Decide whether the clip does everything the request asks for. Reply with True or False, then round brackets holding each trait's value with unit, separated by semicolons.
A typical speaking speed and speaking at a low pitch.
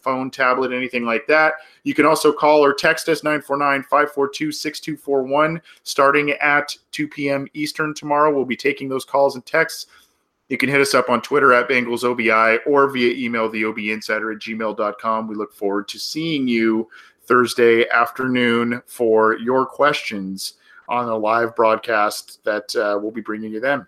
True (160 wpm; 130 Hz)